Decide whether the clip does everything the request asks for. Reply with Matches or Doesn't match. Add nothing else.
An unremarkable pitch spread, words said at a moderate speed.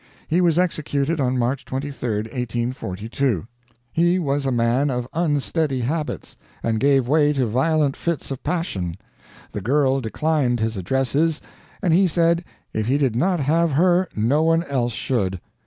Matches